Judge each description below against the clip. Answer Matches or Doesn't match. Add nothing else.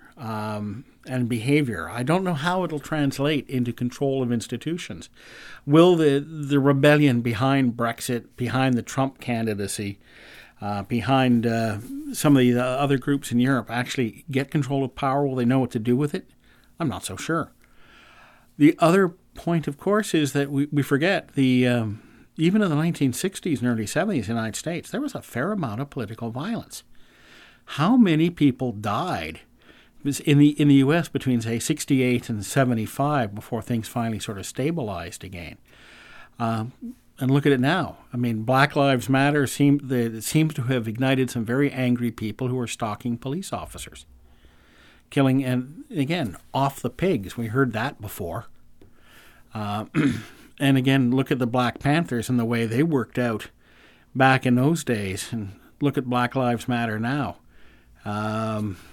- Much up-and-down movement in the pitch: Doesn't match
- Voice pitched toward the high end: Doesn't match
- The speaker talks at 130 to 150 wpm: Doesn't match